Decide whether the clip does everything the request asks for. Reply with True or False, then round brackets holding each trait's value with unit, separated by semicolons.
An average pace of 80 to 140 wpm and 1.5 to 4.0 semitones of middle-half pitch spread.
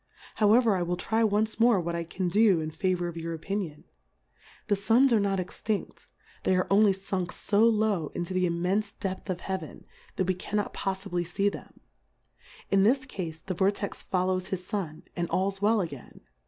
False (185 wpm; 2.9 semitones)